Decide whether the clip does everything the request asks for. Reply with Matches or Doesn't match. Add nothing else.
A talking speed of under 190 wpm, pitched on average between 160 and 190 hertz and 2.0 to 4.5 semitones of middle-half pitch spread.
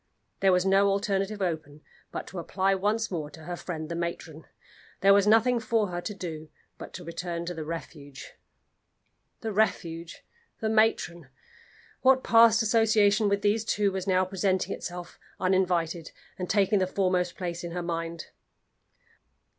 Matches